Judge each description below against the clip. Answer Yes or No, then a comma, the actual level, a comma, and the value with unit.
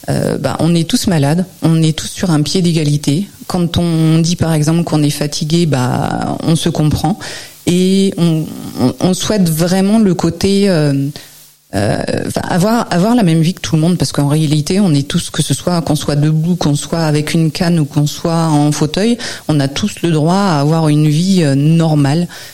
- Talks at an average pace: Yes, average, 200 wpm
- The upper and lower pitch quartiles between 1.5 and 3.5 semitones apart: Yes, average, 2.9 semitones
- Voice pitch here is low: No, medium, 160 Hz